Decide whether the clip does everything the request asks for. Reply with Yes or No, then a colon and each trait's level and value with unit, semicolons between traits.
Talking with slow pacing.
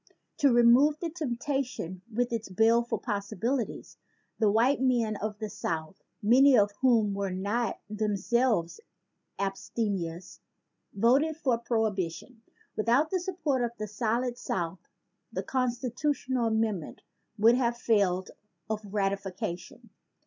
Yes: slow, 120 wpm